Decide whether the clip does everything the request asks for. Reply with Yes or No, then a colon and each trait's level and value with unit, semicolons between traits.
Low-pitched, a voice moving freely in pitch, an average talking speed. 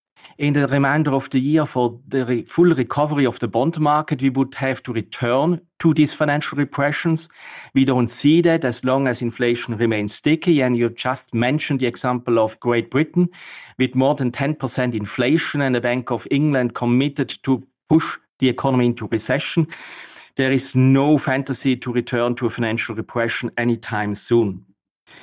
No: low, 130 Hz; average, 3.2 semitones; average, 170 wpm